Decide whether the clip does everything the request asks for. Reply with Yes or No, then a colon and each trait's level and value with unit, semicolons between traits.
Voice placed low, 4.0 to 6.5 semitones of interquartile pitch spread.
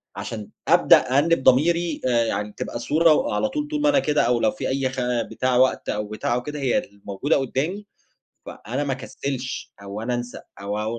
Yes: low, 130 Hz; average, 4.6 semitones